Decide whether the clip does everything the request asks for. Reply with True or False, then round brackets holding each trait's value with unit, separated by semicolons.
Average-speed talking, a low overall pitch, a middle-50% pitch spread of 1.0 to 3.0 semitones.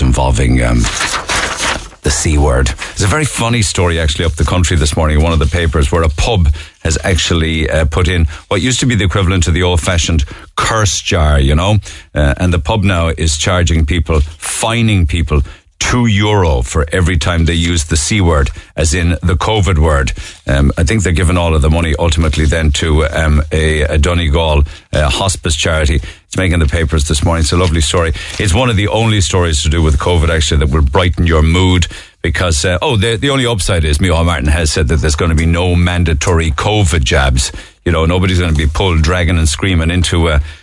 False (210 wpm; 85 Hz; 2.6 semitones)